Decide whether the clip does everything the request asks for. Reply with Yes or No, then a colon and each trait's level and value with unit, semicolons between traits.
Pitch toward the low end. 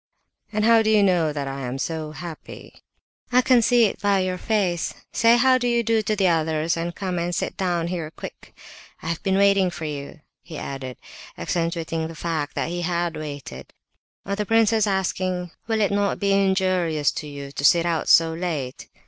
No: medium, 175 Hz